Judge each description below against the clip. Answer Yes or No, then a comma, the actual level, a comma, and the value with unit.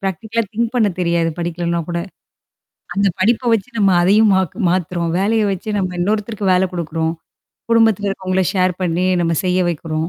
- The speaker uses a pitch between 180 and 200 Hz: Yes, medium, 185 Hz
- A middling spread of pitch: Yes, average, 3.4 semitones